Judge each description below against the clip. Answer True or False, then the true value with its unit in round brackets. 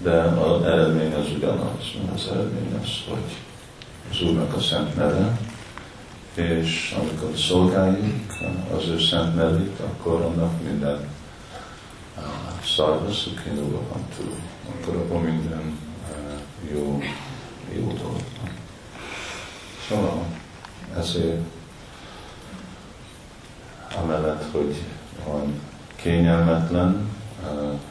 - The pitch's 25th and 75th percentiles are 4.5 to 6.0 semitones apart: False (3.0 semitones)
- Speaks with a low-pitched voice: True (85 Hz)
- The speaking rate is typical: False (85 wpm)